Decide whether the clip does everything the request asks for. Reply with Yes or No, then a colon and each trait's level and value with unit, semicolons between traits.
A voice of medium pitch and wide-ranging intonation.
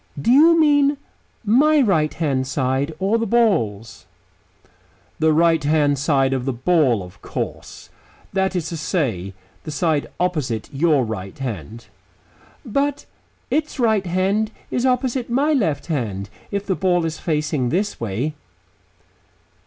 Yes: medium, 160 Hz; wide, 8.3 semitones